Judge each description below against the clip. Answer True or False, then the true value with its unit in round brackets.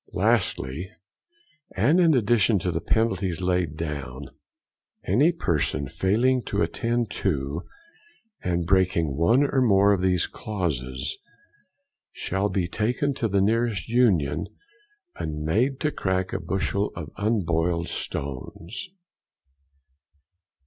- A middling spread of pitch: False (5.7 semitones)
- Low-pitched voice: True (95 Hz)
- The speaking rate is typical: False (120 wpm)